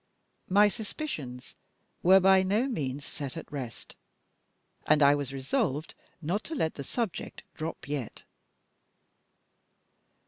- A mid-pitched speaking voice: Yes, medium, 155 Hz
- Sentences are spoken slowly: Yes, slow, 115 wpm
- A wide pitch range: Yes, wide, 6.0 semitones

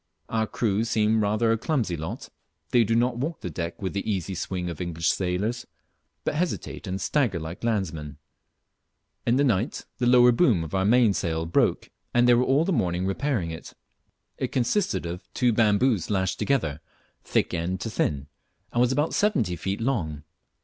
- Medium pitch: No, low, 105 Hz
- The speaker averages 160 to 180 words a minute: Yes, average, 175 wpm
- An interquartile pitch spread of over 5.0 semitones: Yes, wide, 5.6 semitones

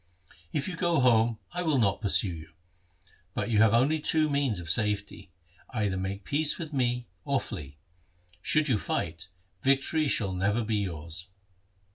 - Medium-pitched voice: No, low, 115 Hz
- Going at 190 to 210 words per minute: No, average, 160 wpm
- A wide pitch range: Yes, wide, 6.5 semitones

